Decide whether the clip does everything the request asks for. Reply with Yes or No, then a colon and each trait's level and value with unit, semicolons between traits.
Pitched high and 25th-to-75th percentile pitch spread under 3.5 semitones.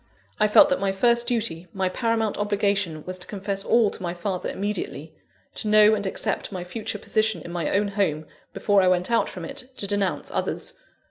Yes: high, 200 Hz; average, 2.8 semitones